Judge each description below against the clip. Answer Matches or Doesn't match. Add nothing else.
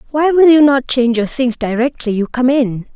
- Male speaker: Doesn't match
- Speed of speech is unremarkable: Doesn't match